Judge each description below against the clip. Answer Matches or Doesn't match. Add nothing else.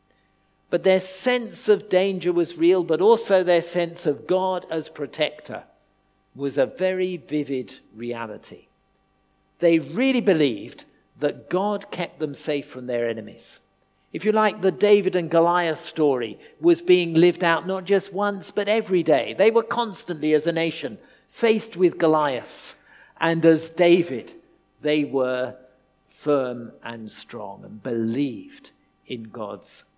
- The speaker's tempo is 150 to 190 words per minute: Doesn't match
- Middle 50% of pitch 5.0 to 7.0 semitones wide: Matches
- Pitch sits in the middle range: Matches